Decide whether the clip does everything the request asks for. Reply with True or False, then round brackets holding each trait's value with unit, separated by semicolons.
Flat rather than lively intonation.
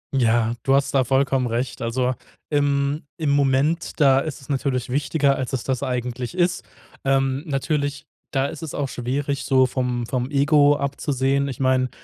True (1.9 semitones)